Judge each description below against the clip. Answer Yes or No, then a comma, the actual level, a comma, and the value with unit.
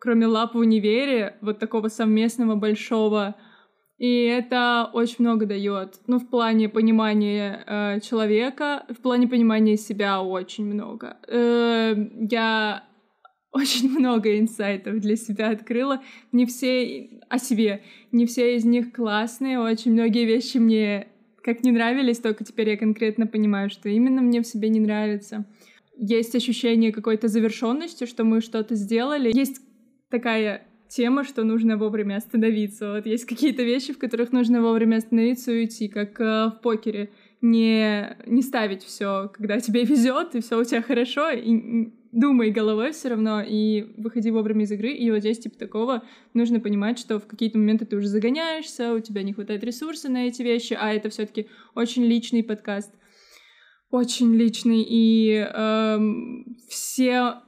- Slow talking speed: No, average, 155 wpm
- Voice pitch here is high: Yes, high, 225 Hz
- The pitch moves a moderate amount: No, narrow, 1.9 semitones